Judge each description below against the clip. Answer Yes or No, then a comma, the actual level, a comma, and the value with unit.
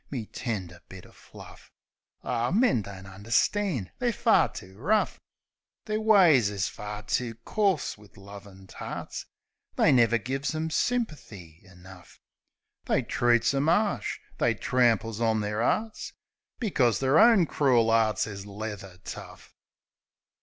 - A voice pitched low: Yes, low, 115 Hz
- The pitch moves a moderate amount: No, wide, 7.9 semitones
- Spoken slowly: Yes, slow, 130 wpm